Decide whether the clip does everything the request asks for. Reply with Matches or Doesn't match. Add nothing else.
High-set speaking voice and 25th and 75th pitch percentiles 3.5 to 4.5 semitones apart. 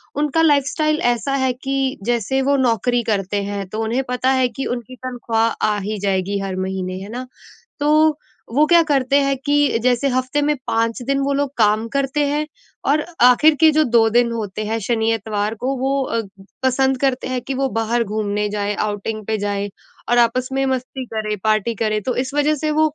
Matches